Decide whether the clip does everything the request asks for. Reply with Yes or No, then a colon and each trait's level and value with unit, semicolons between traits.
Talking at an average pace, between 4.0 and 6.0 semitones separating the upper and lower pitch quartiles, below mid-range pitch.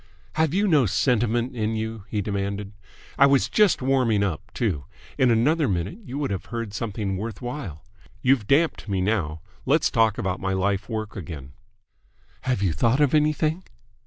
Yes: average, 165 wpm; wide, 5.5 semitones; low, 110 Hz